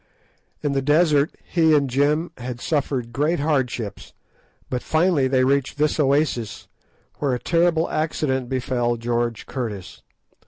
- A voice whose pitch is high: No, medium, 140 Hz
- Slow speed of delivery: Yes, slow, 130 wpm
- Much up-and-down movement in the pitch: No, average, 3.7 semitones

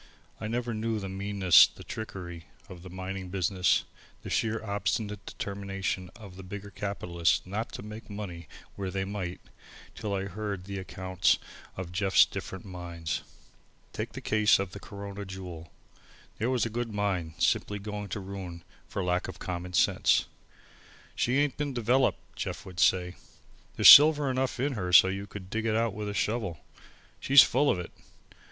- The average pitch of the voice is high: No, low, 100 Hz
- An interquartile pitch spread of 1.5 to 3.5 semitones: Yes, average, 2.8 semitones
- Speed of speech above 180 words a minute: No, average, 170 wpm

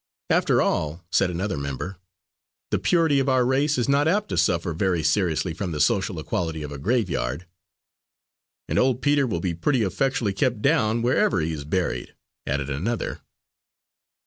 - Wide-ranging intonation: Yes, wide, 7.9 semitones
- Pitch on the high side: No, very low, 95 Hz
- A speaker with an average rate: Yes, average, 165 wpm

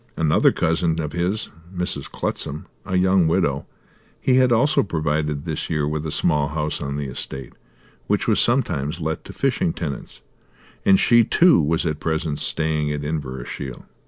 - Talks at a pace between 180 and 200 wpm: No, average, 160 wpm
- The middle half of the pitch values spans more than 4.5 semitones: No, average, 3.4 semitones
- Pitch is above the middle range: No, very low, 80 Hz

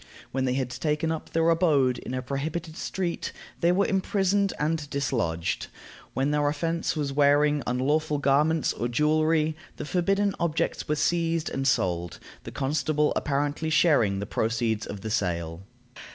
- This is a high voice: No, medium, 150 Hz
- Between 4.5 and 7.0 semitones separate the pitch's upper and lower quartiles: No, average, 4.1 semitones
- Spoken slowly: No, average, 150 wpm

